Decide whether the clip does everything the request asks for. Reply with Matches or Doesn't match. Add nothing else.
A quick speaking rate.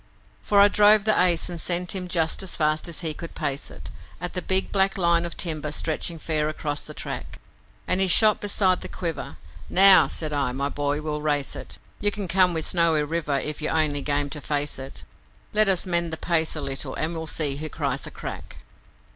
Matches